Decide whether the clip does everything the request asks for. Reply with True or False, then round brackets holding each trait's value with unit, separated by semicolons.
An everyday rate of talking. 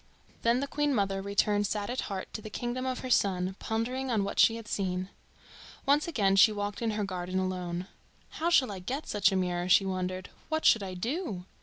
False (210 wpm)